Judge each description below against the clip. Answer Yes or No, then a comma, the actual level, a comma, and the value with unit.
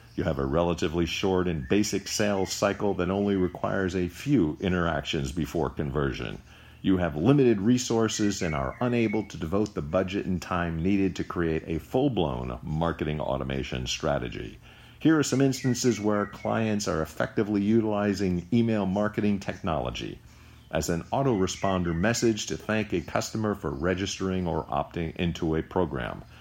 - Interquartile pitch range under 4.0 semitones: No, average, 4.5 semitones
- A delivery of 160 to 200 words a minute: No, average, 150 wpm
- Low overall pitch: Yes, very low, 95 Hz